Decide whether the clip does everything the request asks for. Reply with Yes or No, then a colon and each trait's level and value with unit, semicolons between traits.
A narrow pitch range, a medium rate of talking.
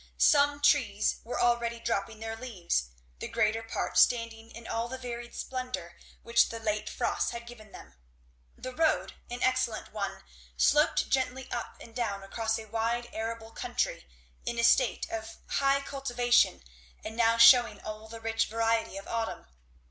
Yes: narrow, 1.6 semitones; average, 160 wpm